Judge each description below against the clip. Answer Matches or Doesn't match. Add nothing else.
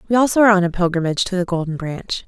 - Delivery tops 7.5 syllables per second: Matches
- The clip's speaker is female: Matches